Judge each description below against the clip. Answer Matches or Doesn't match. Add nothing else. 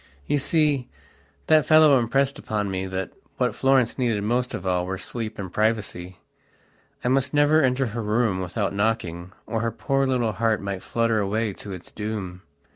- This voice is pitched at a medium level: Doesn't match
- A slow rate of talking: Doesn't match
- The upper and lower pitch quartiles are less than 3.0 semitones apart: Doesn't match